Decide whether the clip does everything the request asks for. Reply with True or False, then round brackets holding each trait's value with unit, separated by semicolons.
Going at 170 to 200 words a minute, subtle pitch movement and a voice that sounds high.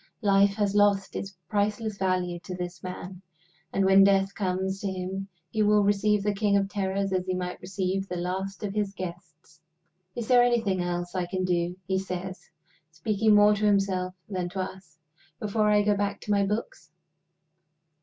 True (180 wpm; 2.0 semitones; 195 Hz)